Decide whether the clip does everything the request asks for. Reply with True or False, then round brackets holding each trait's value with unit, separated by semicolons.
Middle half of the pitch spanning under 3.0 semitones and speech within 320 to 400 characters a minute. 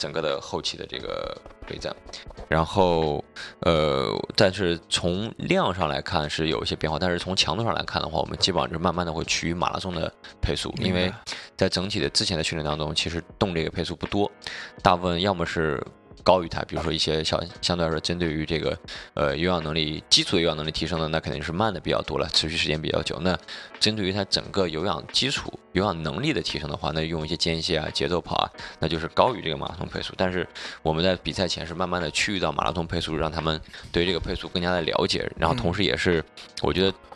True (2.6 semitones; 350 characters per minute)